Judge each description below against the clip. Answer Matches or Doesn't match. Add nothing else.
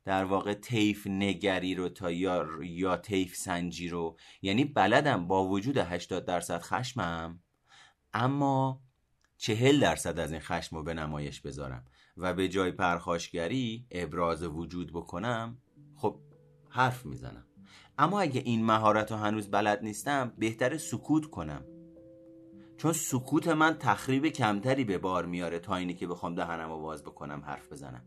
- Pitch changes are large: Matches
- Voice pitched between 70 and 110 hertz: Matches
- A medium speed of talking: Matches